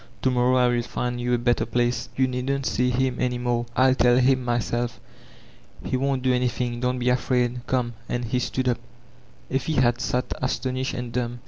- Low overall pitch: Yes, low, 125 Hz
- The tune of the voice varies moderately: No, narrow, 1.0 semitones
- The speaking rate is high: No, average, 190 wpm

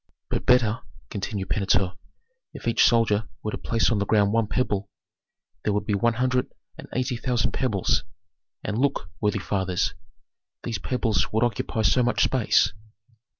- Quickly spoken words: No, average, 155 wpm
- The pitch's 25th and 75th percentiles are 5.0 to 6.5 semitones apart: No, average, 3.0 semitones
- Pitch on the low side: Yes, low, 110 Hz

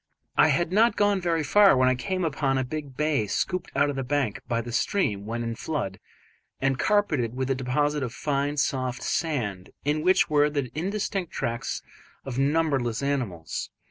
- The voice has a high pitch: No, medium, 140 Hz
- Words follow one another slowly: No, average, 180 wpm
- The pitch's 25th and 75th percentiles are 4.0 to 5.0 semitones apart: Yes, average, 4.3 semitones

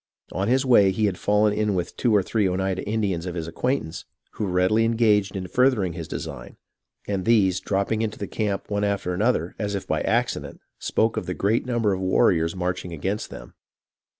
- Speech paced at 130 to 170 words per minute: No, average, 200 wpm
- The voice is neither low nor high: No, low, 100 Hz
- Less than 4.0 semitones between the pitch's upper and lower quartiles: Yes, average, 2.9 semitones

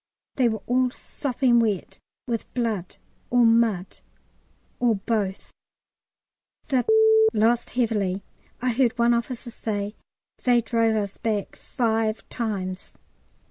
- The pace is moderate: No, slow, 110 wpm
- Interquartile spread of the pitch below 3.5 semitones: Yes, narrow, 2.5 semitones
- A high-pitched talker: Yes, high, 230 Hz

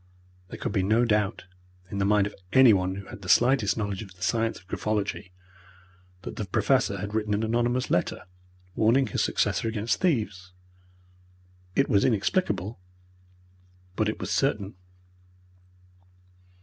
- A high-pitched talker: No, low, 105 Hz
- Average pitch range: Yes, average, 3.0 semitones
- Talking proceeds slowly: No, average, 145 wpm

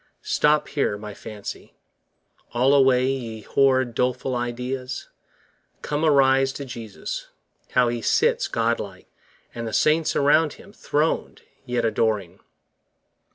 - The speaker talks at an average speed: No, slow, 125 wpm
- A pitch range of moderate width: Yes, average, 3.2 semitones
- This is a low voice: Yes, low, 125 Hz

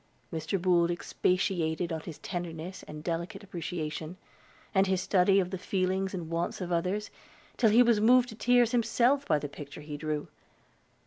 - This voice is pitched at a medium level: Yes, medium, 180 Hz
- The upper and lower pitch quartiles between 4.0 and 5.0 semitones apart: No, average, 3.5 semitones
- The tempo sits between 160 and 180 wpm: Yes, average, 170 wpm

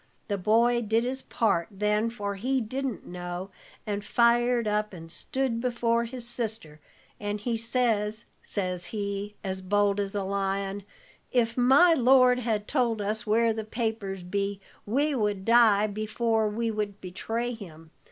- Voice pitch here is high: Yes, high, 215 Hz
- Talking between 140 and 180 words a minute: Yes, average, 150 wpm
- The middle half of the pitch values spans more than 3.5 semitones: No, average, 2.8 semitones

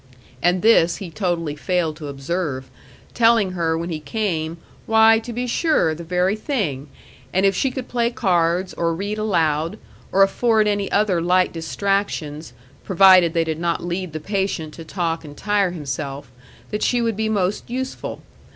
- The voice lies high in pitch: No, medium, 180 Hz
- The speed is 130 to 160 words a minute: No, average, 170 wpm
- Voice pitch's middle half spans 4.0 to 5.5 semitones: Yes, average, 4.5 semitones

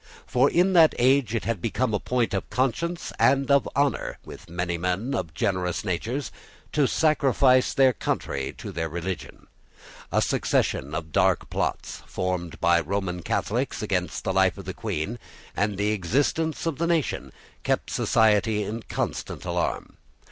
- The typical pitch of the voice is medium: No, low, 110 Hz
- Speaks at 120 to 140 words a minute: No, average, 155 wpm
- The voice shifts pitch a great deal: Yes, wide, 6.9 semitones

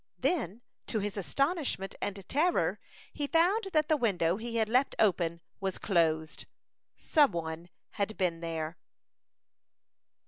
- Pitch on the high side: Yes, high, 205 Hz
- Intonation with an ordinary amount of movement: No, wide, 8.7 semitones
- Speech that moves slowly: Yes, slow, 130 wpm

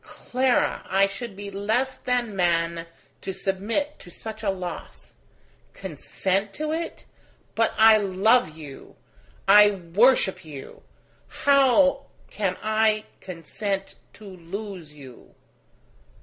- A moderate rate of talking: No, slow, 110 wpm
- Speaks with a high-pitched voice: Yes, high, 200 Hz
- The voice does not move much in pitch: No, average, 3.7 semitones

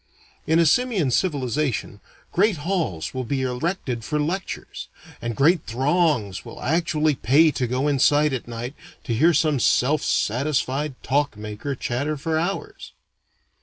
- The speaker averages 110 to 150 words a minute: Yes, average, 140 wpm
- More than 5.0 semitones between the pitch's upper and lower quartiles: No, average, 4.3 semitones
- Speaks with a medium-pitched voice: Yes, medium, 145 Hz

